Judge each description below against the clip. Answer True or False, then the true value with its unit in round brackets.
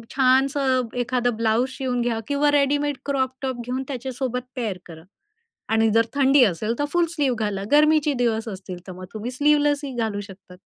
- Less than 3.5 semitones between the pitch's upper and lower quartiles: False (4.1 semitones)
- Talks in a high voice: True (255 Hz)